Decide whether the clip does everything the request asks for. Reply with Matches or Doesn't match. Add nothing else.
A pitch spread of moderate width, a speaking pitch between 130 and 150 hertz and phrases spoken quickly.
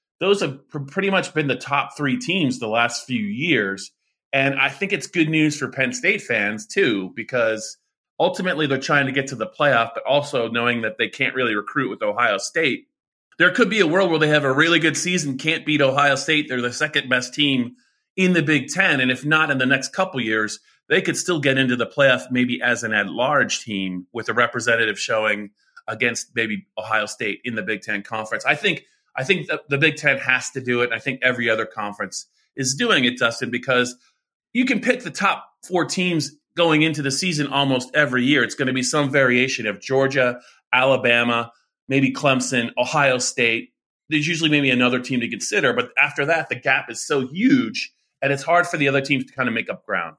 Matches